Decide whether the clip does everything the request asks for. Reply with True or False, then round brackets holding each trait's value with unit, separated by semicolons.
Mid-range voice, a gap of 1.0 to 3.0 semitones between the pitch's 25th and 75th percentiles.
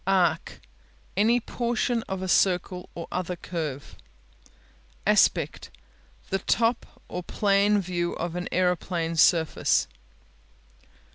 True (180 Hz; 2.7 semitones)